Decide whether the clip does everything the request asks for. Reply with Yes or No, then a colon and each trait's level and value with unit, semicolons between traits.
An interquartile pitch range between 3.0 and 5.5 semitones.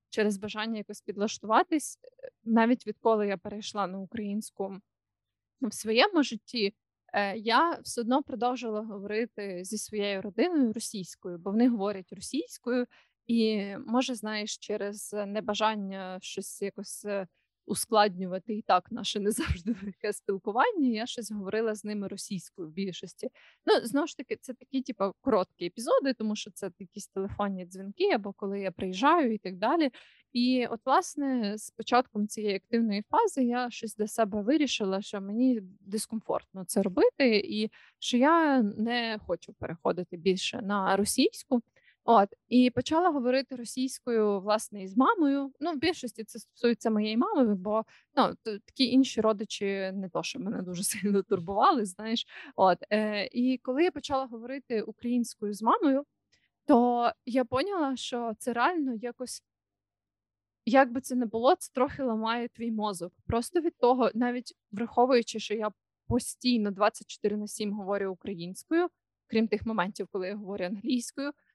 Yes: average, 3.9 semitones